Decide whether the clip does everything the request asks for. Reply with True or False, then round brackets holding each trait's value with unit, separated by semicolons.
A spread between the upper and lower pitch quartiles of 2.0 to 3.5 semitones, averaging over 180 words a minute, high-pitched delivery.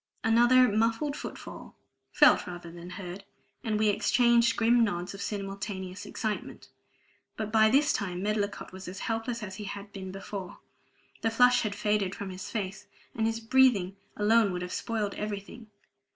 False (2.7 semitones; 165 wpm; 210 Hz)